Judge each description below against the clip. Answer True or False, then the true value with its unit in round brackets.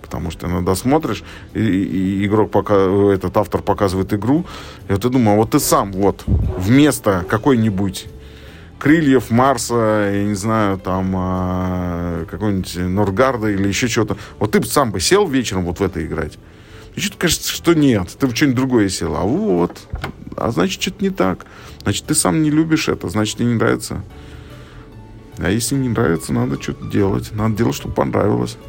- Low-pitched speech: True (105 Hz)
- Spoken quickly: True (175 wpm)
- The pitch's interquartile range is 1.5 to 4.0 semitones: False (4.6 semitones)